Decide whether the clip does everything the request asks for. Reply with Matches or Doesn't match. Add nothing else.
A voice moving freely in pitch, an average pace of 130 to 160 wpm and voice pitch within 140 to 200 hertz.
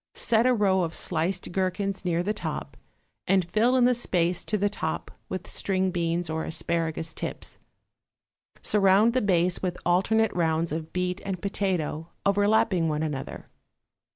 Doesn't match